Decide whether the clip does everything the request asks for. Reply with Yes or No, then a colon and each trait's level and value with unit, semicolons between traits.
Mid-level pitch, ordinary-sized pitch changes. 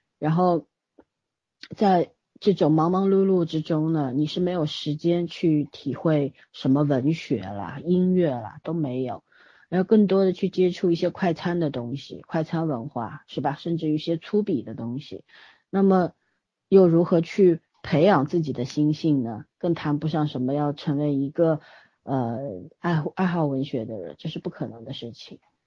Yes: medium, 160 Hz; average, 3.9 semitones